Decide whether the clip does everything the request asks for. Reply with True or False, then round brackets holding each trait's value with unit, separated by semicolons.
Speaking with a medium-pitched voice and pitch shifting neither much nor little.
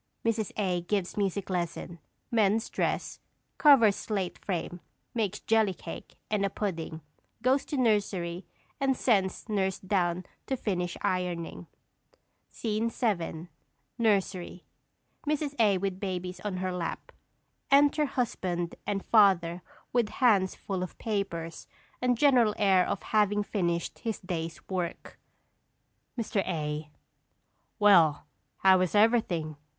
False (195 Hz; 3.7 semitones)